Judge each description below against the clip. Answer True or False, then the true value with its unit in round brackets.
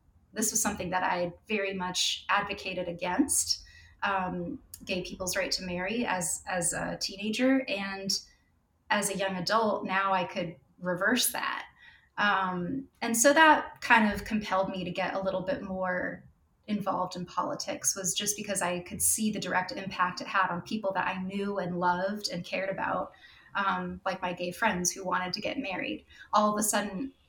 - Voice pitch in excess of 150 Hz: True (190 Hz)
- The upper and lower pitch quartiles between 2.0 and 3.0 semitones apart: True (2.6 semitones)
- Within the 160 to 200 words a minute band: True (180 wpm)